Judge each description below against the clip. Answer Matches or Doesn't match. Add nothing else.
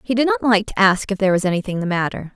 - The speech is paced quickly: Matches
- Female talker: Matches